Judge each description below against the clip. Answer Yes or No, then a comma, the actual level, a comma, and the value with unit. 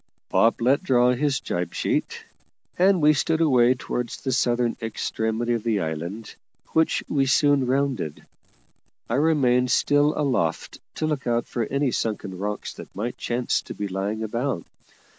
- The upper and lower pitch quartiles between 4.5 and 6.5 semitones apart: No, average, 4.0 semitones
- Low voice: Yes, low, 125 Hz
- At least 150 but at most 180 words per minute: Yes, average, 155 wpm